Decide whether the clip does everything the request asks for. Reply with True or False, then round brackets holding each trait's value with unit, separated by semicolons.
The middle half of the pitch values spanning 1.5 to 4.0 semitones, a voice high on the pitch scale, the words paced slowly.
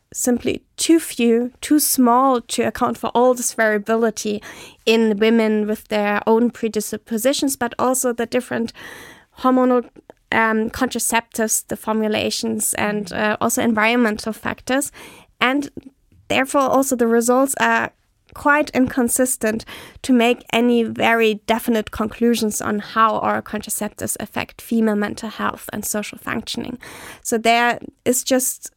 True (2.5 semitones; 235 Hz; 125 wpm)